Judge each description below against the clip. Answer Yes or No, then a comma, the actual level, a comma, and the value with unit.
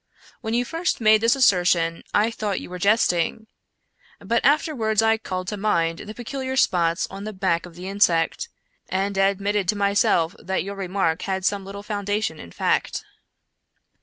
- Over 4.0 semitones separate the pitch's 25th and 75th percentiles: No, average, 3.0 semitones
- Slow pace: No, average, 165 wpm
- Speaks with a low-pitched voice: No, high, 200 Hz